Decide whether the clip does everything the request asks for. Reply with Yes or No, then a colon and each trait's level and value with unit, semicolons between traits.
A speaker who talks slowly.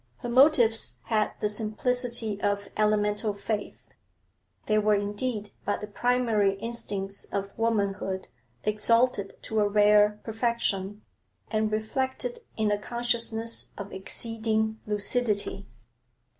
Yes: slow, 110 wpm